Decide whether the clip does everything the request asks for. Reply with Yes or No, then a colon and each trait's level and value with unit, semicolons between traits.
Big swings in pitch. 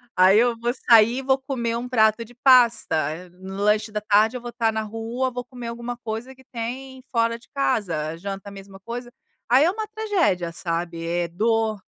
No: average, 3.6 semitones